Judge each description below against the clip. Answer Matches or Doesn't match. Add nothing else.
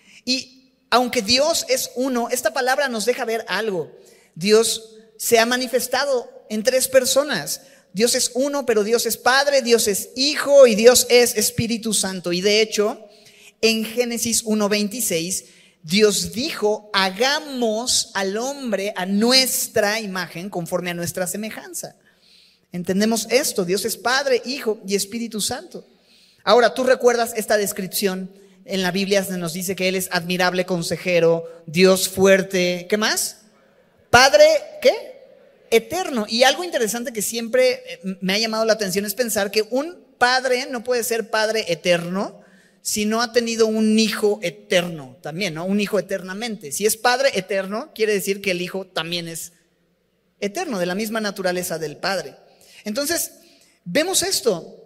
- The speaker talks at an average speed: Matches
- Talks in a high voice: Matches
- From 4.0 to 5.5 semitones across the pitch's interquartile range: Matches